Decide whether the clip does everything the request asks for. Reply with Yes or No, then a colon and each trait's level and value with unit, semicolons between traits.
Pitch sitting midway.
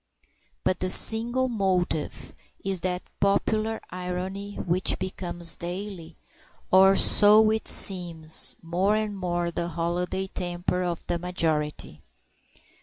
Yes: medium, 180 Hz